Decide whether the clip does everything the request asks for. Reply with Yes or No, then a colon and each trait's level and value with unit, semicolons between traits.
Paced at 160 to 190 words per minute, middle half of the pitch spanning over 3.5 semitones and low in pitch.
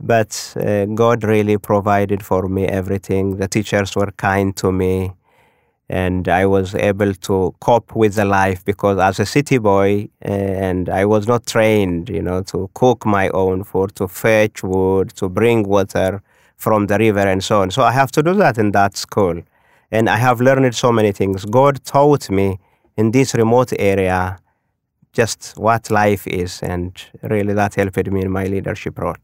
No: average, 185 wpm; narrow, 2.5 semitones; low, 100 Hz